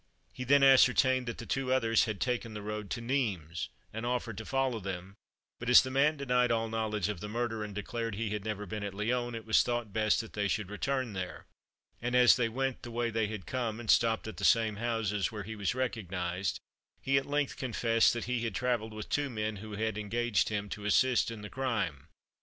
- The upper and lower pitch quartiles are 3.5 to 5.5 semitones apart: No, average, 2.9 semitones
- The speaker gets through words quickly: Yes, fast, 225 wpm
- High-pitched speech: No, low, 115 Hz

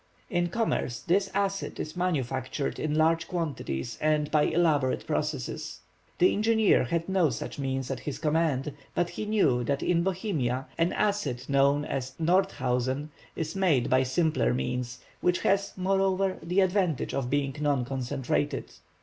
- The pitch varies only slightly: No, wide, 5.5 semitones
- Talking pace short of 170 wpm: Yes, average, 150 wpm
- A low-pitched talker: No, medium, 155 Hz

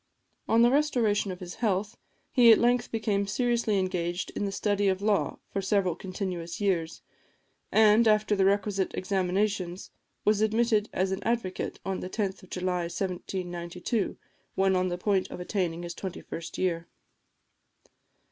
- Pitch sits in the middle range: No, high, 195 Hz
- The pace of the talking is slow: No, average, 155 wpm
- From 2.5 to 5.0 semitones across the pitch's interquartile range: Yes, average, 2.8 semitones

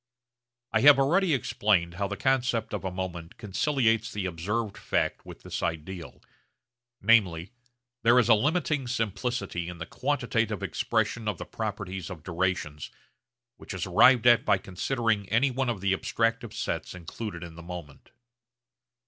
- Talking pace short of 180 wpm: Yes, average, 150 wpm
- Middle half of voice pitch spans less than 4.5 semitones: No, average, 4.9 semitones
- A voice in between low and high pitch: No, low, 105 Hz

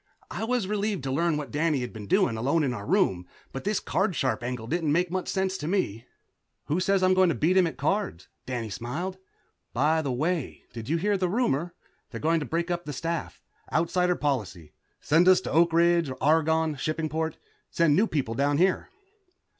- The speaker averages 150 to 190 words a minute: No, average, 200 wpm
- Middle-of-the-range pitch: Yes, medium, 160 Hz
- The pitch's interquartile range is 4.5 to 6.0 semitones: Yes, average, 4.8 semitones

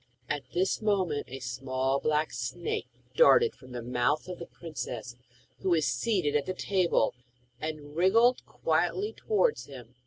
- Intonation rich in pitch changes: Yes, wide, 6.4 semitones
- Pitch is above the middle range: No, medium, 155 Hz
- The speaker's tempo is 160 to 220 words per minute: No, average, 150 wpm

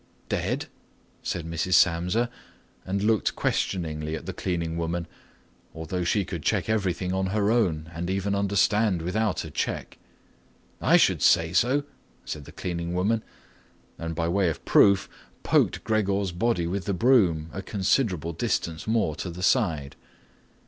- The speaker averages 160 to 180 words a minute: No, average, 150 wpm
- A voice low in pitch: Yes, very low, 90 Hz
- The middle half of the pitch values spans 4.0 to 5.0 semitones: No, average, 3.4 semitones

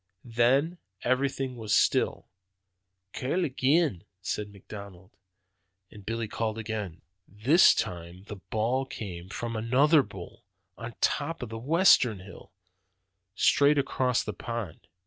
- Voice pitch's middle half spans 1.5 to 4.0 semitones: No, average, 4.6 semitones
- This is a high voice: No, low, 115 Hz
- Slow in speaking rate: Yes, slow, 120 wpm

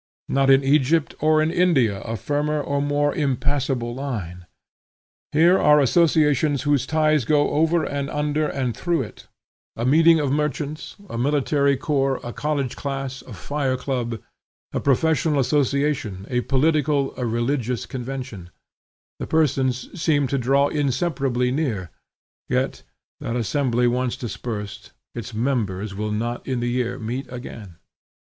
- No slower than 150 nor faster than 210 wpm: No, average, 140 wpm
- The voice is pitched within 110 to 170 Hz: Yes, low, 135 Hz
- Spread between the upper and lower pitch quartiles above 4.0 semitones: No, average, 3.5 semitones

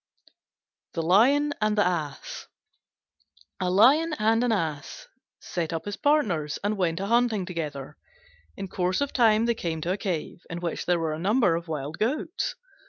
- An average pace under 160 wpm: No, average, 170 wpm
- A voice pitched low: No, high, 190 Hz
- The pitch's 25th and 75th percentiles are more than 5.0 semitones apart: Yes, wide, 5.6 semitones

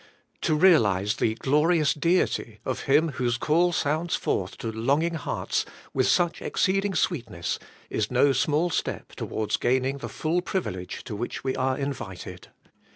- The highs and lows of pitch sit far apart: Yes, wide, 5.9 semitones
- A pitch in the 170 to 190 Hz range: No, medium, 140 Hz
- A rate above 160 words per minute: No, average, 150 wpm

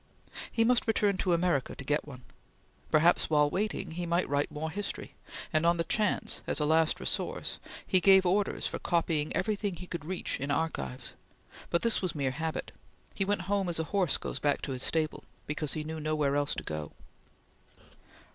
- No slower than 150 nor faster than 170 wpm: No, average, 190 wpm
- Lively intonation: No, average, 4.0 semitones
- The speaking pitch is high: No, medium, 165 Hz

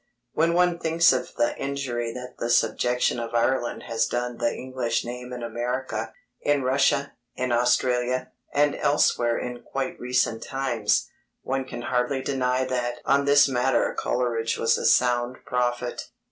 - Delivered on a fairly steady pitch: Yes, narrow, 1.8 semitones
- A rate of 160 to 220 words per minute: No, average, 150 wpm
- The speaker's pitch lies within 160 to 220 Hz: No, low, 125 Hz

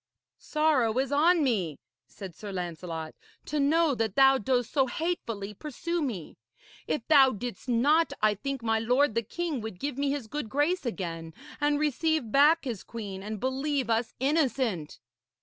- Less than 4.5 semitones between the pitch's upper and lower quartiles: No, wide, 5.4 semitones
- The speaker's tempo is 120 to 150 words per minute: No, average, 165 wpm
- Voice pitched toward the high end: Yes, very high, 255 Hz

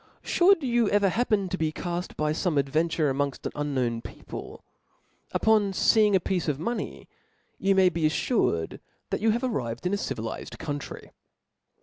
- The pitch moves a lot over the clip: Yes, wide, 6.2 semitones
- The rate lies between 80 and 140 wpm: No, average, 165 wpm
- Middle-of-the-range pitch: Yes, medium, 175 Hz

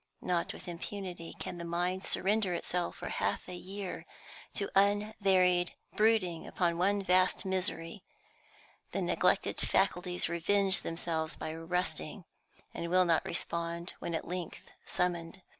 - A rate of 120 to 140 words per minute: Yes, slow, 135 wpm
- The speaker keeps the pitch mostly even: Yes, narrow, 2.1 semitones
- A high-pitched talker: No, medium, 180 Hz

